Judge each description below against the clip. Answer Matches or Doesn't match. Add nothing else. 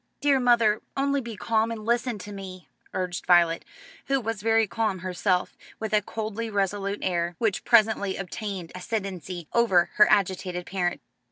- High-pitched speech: Matches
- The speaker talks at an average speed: Matches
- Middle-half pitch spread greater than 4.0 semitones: Doesn't match